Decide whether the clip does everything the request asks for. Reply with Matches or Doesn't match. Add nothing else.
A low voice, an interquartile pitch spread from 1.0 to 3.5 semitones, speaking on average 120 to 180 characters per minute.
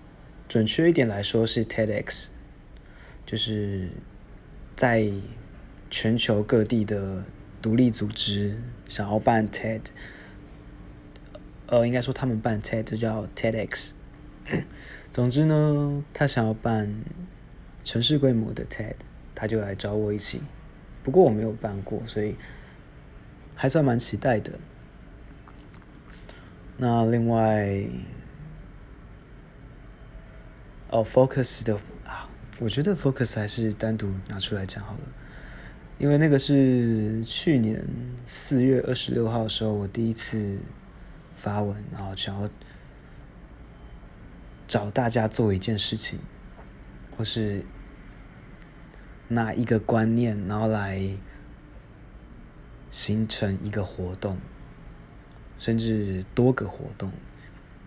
Matches